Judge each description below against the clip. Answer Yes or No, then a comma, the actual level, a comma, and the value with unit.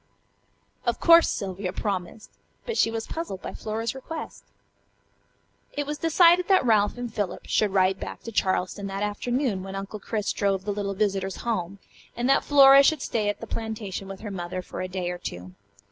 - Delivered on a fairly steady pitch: No, average, 4.2 semitones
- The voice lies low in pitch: No, high, 205 Hz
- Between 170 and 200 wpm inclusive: Yes, average, 185 wpm